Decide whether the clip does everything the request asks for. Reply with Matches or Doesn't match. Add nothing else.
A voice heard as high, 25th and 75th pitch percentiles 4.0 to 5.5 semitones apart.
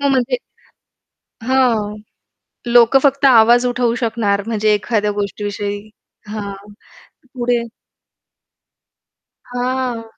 Doesn't match